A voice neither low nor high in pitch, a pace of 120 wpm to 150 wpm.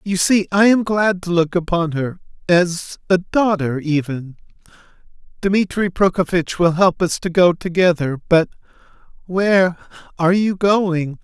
Yes: medium, 180 Hz; average, 140 wpm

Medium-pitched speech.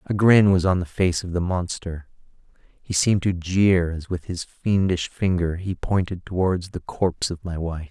No: very low, 90 Hz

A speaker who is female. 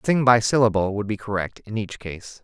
No: male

